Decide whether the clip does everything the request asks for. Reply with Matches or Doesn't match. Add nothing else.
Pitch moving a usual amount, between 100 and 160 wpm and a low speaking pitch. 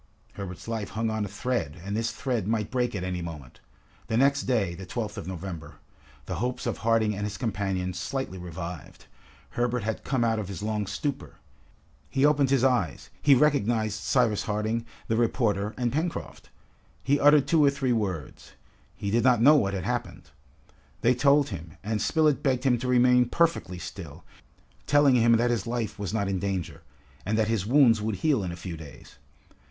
Doesn't match